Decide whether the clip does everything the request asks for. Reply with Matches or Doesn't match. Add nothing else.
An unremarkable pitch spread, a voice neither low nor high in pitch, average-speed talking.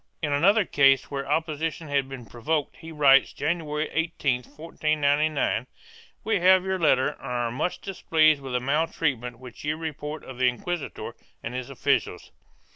Matches